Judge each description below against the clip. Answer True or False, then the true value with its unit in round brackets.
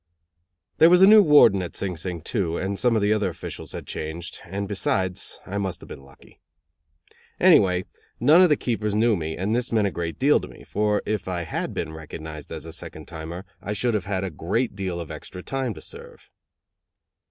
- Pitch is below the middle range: True (95 Hz)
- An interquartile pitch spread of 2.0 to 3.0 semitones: False (4.3 semitones)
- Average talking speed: False (210 wpm)